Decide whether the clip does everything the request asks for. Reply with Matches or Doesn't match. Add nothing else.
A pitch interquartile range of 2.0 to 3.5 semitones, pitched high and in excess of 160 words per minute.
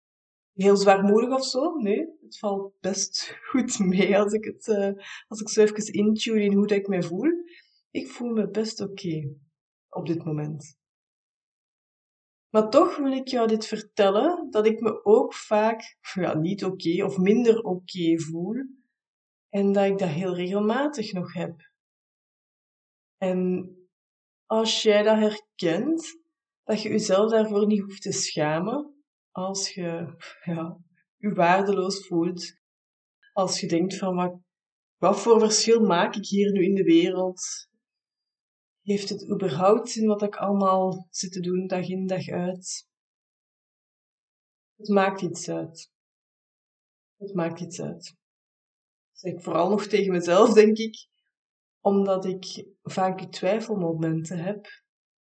Doesn't match